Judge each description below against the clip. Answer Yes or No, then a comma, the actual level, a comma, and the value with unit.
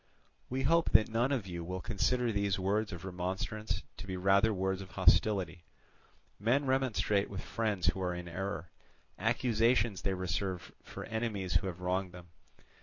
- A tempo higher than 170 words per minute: No, average, 165 wpm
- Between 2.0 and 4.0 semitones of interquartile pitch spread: Yes, average, 3.4 semitones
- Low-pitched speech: Yes, very low, 95 Hz